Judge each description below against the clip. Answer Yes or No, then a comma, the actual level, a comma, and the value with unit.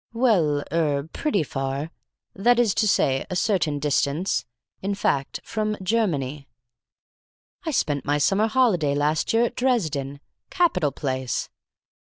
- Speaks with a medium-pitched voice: Yes, medium, 160 Hz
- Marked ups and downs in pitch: Yes, wide, 7.4 semitones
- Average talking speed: No, slow, 130 wpm